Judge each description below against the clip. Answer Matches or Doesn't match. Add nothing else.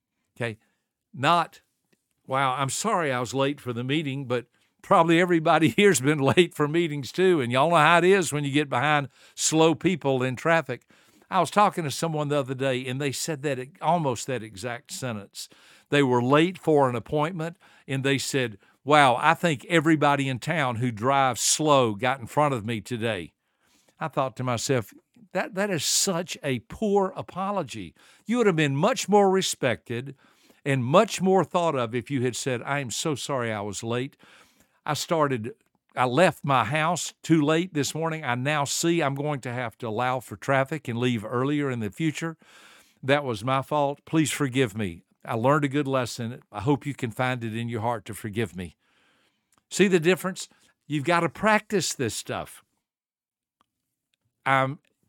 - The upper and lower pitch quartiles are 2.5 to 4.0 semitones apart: Doesn't match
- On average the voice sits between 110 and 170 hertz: Matches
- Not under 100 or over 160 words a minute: Doesn't match